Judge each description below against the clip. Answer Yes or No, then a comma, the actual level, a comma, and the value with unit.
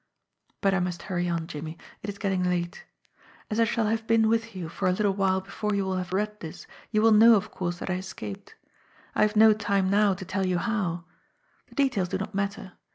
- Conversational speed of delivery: No, fast, 225 wpm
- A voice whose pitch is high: Yes, high, 195 Hz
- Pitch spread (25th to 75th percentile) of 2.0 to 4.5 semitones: Yes, average, 2.7 semitones